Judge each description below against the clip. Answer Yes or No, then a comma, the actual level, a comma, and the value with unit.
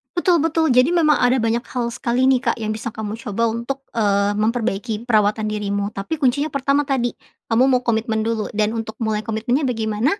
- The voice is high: Yes, high, 230 Hz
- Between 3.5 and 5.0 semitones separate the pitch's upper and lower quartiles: No, average, 3.0 semitones